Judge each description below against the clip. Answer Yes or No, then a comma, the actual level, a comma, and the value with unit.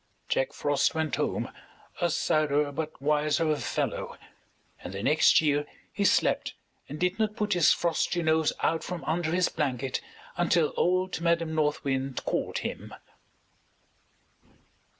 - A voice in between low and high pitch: Yes, medium, 155 Hz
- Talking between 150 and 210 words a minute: No, slow, 135 wpm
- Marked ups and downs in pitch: No, average, 2.9 semitones